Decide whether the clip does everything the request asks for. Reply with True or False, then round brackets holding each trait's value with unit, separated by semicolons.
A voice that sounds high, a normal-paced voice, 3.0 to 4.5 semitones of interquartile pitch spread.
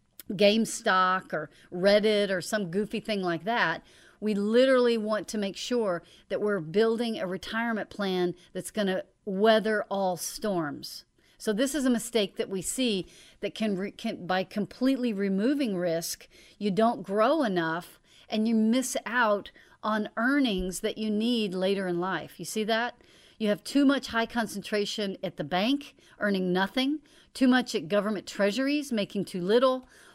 True (210 Hz; 160 wpm; 3.4 semitones)